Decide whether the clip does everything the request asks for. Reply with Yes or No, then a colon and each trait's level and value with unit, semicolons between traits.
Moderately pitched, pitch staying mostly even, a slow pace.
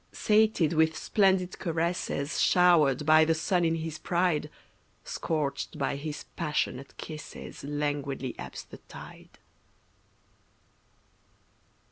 No: medium, 160 Hz; average, 3.0 semitones; slow, 100 wpm